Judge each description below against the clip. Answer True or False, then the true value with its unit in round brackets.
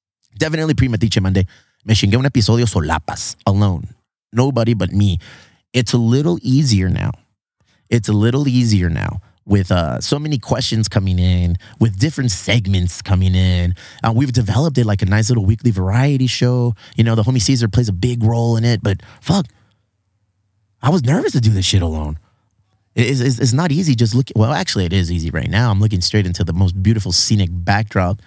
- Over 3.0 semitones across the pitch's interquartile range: True (4.1 semitones)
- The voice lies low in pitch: True (110 Hz)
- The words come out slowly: False (190 wpm)